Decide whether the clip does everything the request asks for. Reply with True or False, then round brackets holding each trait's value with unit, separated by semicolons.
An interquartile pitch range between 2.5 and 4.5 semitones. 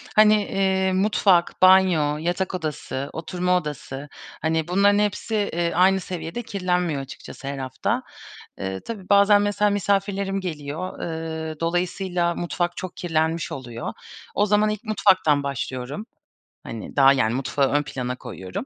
False (4.9 semitones)